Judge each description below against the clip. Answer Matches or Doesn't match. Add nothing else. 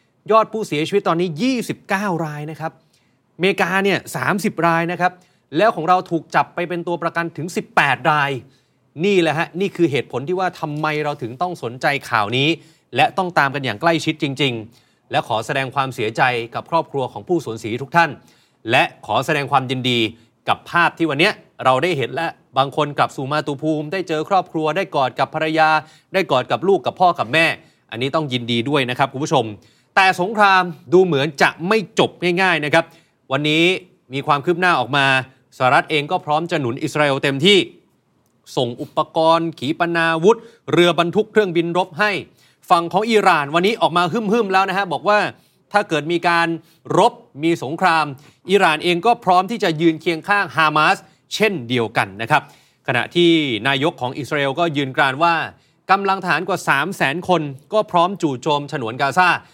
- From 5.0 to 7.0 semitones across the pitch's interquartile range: Doesn't match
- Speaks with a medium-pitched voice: Matches